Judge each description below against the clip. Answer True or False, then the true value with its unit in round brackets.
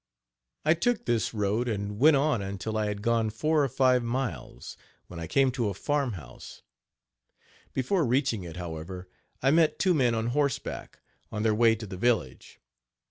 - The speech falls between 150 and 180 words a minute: True (175 wpm)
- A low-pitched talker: True (115 Hz)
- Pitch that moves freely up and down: False (4.9 semitones)